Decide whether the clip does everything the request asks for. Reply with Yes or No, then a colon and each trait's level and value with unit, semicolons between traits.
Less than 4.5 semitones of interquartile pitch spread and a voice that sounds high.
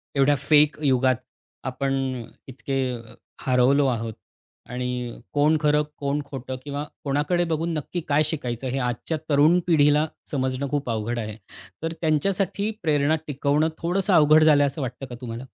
No: average, 3.0 semitones; medium, 140 Hz